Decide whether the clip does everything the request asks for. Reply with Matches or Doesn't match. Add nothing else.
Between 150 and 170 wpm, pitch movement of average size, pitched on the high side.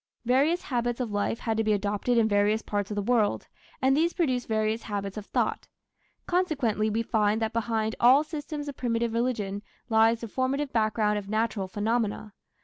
Doesn't match